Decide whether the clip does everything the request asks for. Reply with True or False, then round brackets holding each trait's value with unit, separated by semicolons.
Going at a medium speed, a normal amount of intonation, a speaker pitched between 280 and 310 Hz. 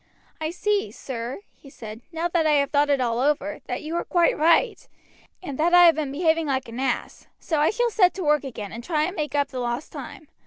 False (240 wpm; 4.3 semitones; 300 Hz)